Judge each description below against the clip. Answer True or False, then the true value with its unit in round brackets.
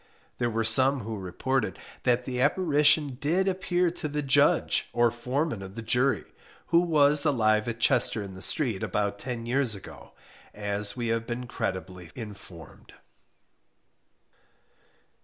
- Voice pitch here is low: True (120 Hz)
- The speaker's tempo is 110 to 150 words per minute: True (140 wpm)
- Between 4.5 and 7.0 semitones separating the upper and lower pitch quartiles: True (5.0 semitones)